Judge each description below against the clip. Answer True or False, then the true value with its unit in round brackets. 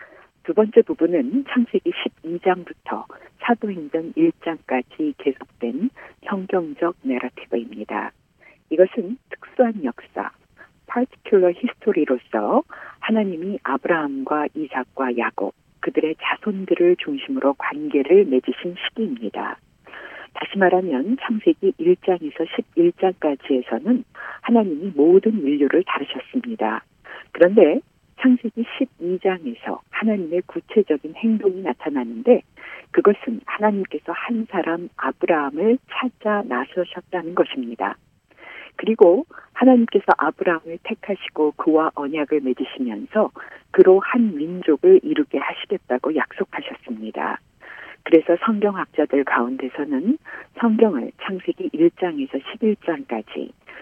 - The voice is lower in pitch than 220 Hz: True (190 Hz)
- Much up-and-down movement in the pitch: True (7.6 semitones)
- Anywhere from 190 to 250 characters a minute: False (270 characters per minute)